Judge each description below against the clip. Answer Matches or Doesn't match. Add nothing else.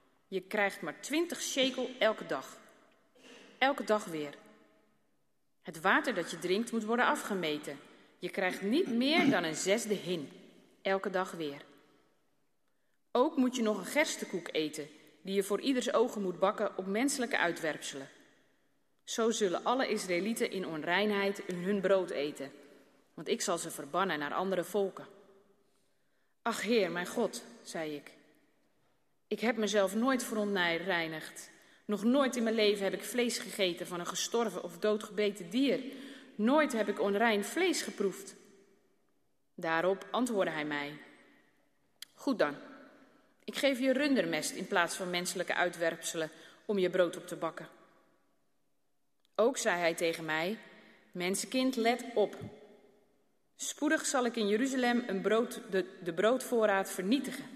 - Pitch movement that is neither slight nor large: Matches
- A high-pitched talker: Matches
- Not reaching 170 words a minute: Matches